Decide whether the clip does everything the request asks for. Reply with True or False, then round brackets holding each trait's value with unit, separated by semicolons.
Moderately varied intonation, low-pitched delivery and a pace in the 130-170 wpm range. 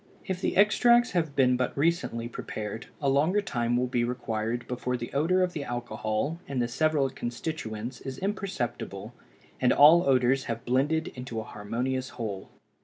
True (4.9 semitones; 125 Hz; 165 wpm)